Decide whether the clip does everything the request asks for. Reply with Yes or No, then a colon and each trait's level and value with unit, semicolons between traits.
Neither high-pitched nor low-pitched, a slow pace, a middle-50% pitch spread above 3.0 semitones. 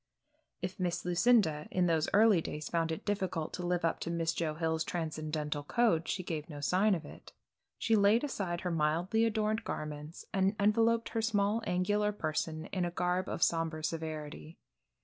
No: medium, 175 Hz; average, 175 wpm; average, 4.3 semitones